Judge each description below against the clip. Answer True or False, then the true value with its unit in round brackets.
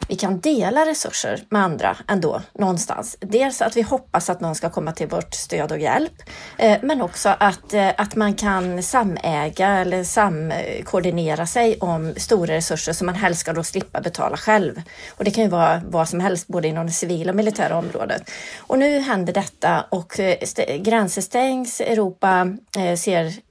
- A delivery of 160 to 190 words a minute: True (170 wpm)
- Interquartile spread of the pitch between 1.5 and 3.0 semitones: False (4.3 semitones)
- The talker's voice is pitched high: True (195 Hz)